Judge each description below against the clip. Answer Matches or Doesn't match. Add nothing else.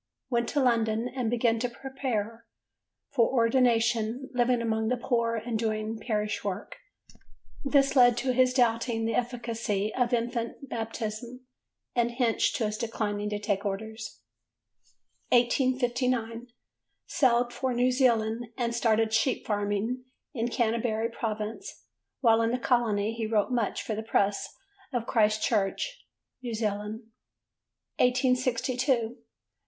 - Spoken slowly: Matches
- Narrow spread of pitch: Matches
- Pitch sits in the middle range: Doesn't match